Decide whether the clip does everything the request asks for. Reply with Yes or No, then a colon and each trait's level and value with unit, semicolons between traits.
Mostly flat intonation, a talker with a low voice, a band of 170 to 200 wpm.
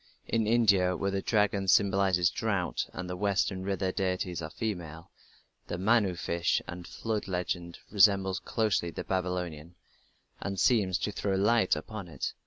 No: narrow, 2.3 semitones; very low, 95 Hz; average, 150 wpm